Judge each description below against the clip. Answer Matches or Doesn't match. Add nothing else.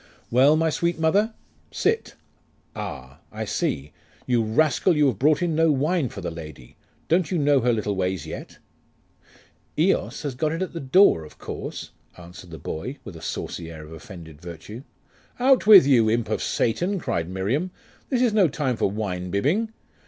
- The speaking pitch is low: Matches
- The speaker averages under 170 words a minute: Doesn't match